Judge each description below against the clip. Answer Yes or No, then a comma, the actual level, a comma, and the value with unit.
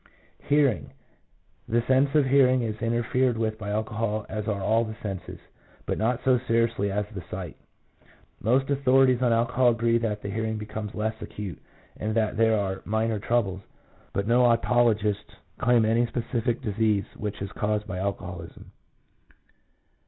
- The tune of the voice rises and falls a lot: No, narrow, 2.4 semitones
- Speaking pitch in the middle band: No, low, 110 Hz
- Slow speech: No, average, 155 wpm